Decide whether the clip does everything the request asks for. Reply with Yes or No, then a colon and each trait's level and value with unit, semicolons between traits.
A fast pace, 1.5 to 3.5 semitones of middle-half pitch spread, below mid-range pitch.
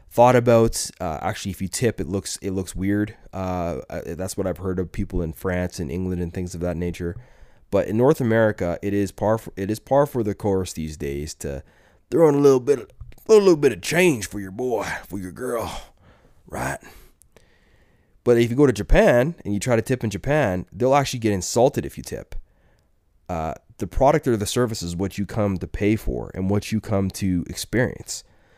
No: fast, 215 wpm; average, 4.7 semitones; low, 100 Hz